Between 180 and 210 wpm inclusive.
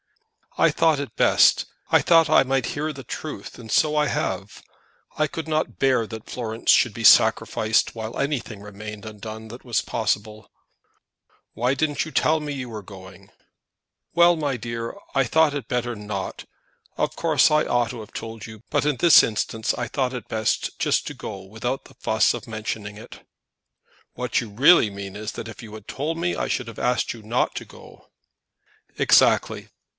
Yes: average, 190 wpm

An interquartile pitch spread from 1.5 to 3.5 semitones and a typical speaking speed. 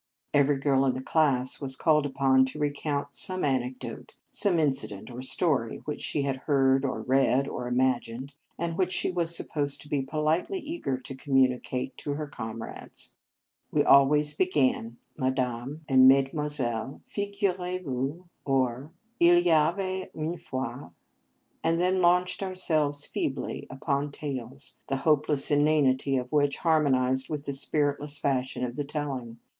Yes: average, 3.0 semitones; average, 155 wpm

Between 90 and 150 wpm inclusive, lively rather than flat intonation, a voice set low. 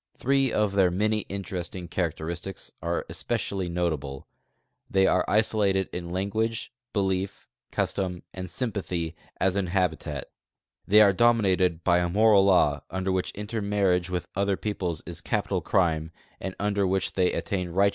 No: average, 145 wpm; narrow, 2.4 semitones; very low, 95 Hz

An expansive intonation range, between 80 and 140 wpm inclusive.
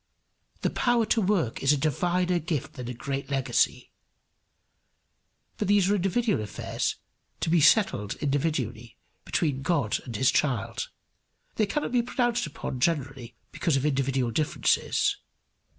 Yes: wide, 6.3 semitones; slow, 135 wpm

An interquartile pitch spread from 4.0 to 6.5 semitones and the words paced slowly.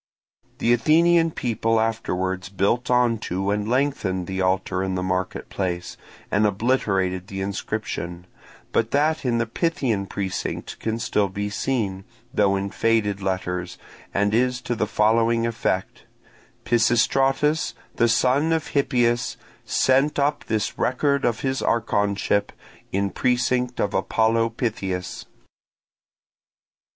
Yes: average, 4.4 semitones; slow, 125 wpm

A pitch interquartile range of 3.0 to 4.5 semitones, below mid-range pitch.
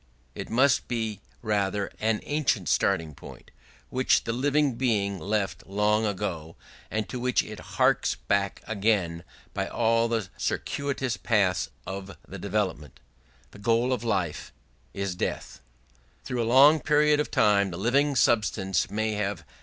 Yes: average, 3.8 semitones; low, 105 Hz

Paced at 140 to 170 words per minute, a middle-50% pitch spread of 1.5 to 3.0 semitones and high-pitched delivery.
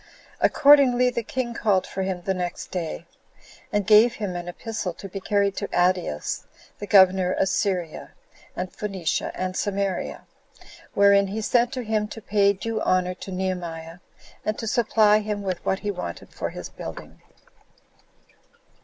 Yes: average, 155 wpm; average, 2.7 semitones; high, 200 Hz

